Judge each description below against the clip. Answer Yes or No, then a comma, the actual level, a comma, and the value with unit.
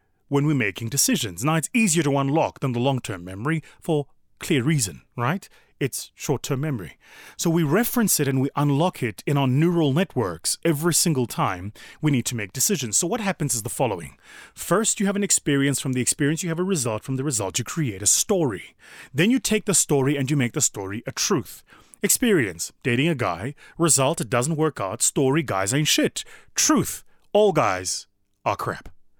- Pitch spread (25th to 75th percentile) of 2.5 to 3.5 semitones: No, wide, 5.4 semitones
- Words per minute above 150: Yes, average, 195 wpm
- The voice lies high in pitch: No, medium, 145 Hz